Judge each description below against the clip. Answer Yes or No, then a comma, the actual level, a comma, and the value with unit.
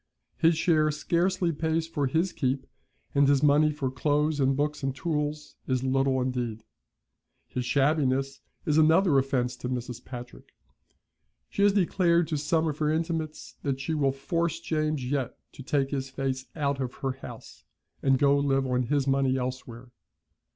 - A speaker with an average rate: Yes, average, 165 wpm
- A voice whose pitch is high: No, medium, 140 Hz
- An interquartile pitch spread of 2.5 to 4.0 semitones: Yes, average, 2.9 semitones